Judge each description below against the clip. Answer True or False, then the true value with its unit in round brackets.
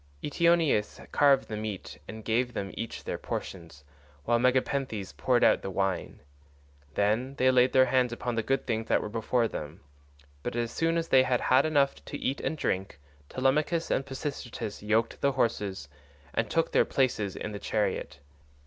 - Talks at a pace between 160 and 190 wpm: True (175 wpm)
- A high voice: False (120 Hz)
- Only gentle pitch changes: False (4.2 semitones)